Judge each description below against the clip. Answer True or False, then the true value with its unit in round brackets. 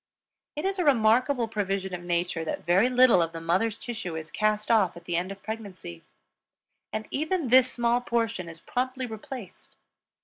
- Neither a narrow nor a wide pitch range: False (5.7 semitones)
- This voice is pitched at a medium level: False (215 Hz)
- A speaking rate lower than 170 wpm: False (175 wpm)